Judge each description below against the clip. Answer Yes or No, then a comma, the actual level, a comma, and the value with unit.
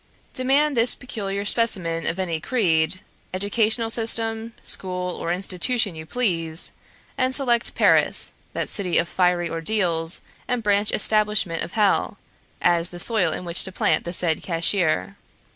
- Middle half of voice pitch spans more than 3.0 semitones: Yes, average, 4.9 semitones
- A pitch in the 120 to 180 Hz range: No, high, 190 Hz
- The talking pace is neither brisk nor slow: Yes, average, 145 wpm